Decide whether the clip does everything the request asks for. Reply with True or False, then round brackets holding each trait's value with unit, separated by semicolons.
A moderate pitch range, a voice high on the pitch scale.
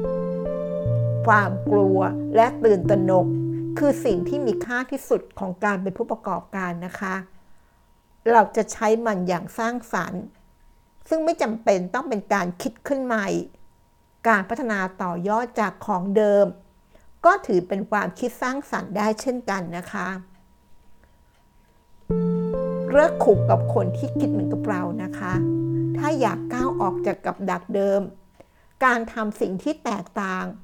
False (7.4 semitones; 195 Hz)